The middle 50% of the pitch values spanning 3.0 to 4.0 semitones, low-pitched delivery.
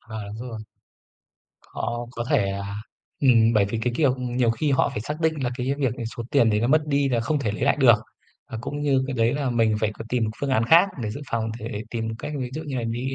Yes: average, 3.5 semitones; low, 120 Hz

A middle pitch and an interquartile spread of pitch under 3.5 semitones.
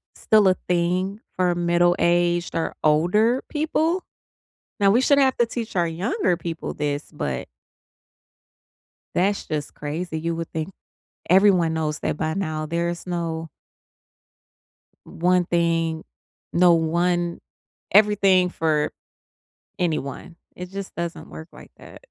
Yes: medium, 175 Hz; average, 2.7 semitones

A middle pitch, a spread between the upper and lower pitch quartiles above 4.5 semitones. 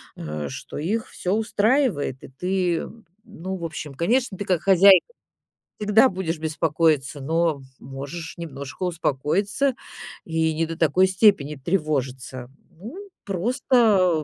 Yes: medium, 170 Hz; average, 4.9 semitones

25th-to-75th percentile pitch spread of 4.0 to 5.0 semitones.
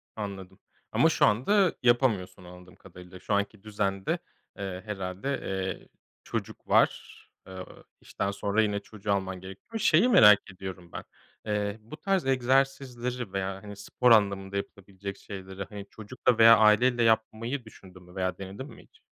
No: average, 3.5 semitones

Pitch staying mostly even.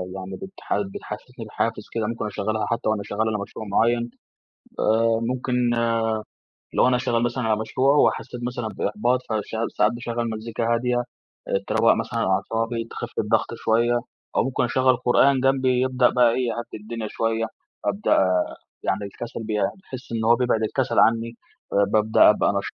Yes: narrow, 2.1 semitones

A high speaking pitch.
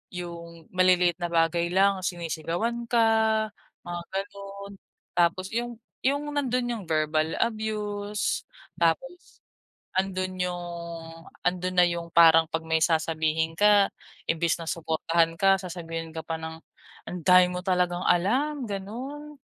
No: medium, 180 Hz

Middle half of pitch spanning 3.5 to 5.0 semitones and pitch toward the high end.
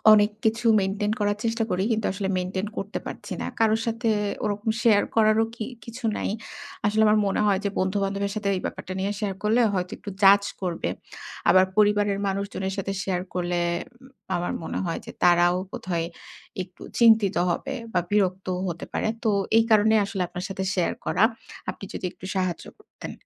No: narrow, 2.5 semitones; high, 200 Hz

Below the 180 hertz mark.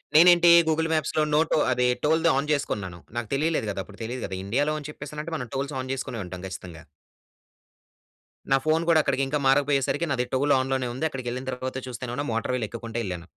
Yes: low, 135 Hz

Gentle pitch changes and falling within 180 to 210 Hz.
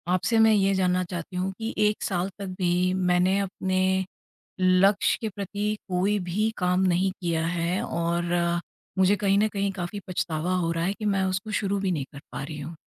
Yes: narrow, 2.3 semitones; medium, 185 Hz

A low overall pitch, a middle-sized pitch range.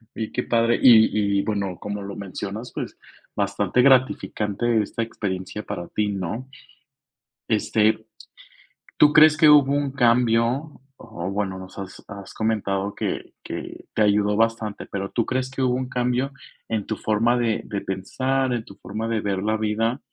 Yes: low, 110 Hz; average, 3.5 semitones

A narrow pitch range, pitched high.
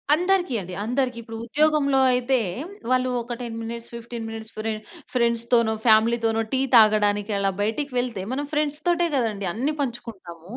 No: average, 3.3 semitones; high, 235 Hz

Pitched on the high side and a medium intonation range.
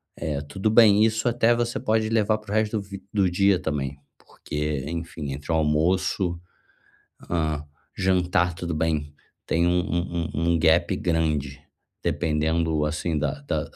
No: very low, 85 Hz; average, 4.3 semitones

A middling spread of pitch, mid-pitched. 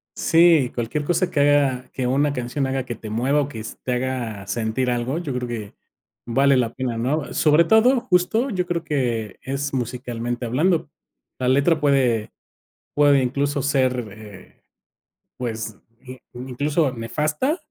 No: average, 3.6 semitones; low, 130 Hz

